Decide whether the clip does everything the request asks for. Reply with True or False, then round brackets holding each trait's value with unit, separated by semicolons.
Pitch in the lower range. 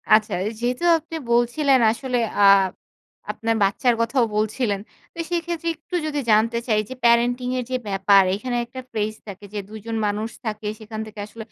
False (230 Hz)